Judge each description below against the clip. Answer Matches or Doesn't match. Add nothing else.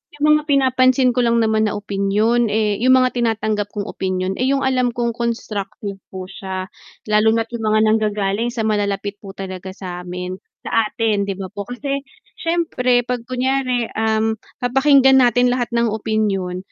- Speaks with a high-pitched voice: Matches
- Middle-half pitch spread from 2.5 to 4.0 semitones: Matches